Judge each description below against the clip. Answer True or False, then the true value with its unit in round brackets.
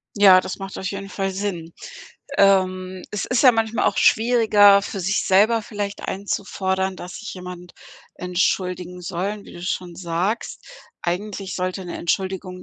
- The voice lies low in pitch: False (190 Hz)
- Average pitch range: False (2.0 semitones)